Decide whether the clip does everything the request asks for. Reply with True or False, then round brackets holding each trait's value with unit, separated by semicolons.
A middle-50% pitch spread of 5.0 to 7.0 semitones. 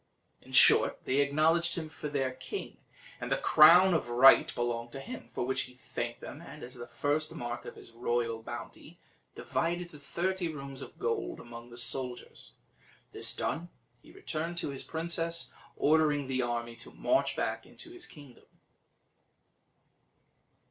True (5.6 semitones)